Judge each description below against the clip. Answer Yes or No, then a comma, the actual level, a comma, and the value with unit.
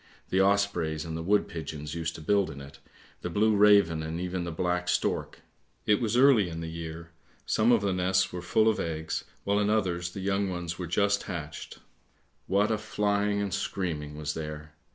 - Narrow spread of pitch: No, average, 3.9 semitones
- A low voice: Yes, very low, 90 Hz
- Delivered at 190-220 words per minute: Yes, average, 195 wpm